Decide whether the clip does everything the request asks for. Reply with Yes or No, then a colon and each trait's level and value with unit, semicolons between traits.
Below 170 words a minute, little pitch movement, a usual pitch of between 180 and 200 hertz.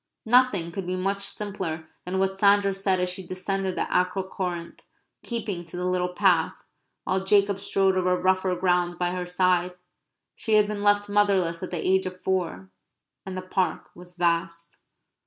No: average, 175 wpm; narrow, 1.7 semitones; medium, 185 Hz